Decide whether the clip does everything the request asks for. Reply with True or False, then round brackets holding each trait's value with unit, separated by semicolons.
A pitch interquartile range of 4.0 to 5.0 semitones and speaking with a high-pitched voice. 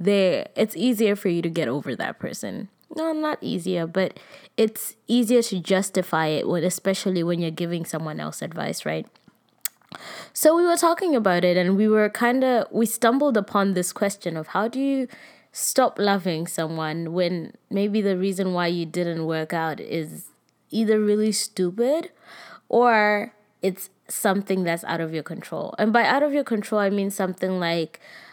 True (4.5 semitones; 195 Hz)